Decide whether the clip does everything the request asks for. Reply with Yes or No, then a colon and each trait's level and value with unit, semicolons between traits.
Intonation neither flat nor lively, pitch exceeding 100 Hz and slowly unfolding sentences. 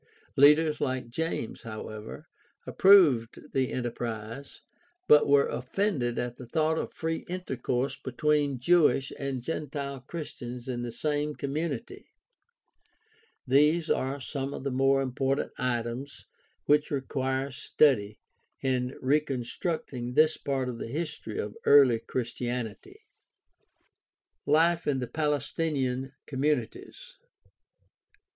Yes: average, 3.3 semitones; low, 135 Hz; slow, 110 wpm